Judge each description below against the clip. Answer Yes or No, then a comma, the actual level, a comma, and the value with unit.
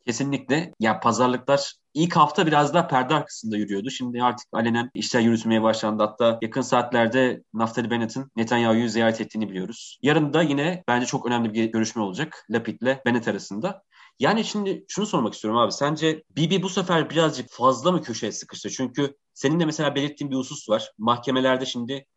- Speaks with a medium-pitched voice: No, low, 125 Hz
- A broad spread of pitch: No, average, 4.3 semitones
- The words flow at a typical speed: No, fast, 175 wpm